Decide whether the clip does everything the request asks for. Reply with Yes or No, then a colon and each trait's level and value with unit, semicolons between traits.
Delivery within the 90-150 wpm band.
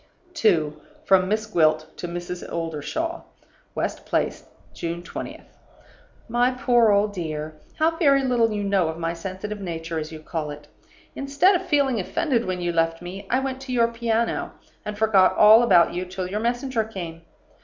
No: average, 170 wpm